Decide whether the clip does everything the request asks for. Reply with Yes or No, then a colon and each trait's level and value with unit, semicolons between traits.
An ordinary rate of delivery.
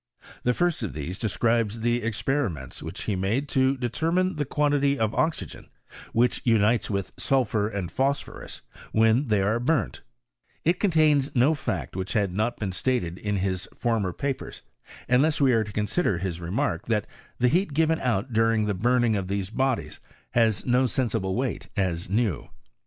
Yes: average, 165 wpm